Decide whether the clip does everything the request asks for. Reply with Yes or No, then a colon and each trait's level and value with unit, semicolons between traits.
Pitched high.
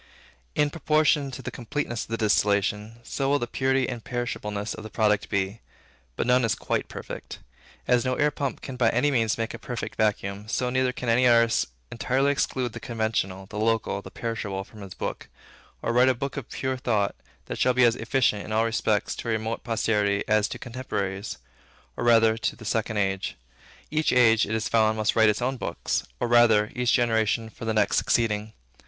No: low, 115 Hz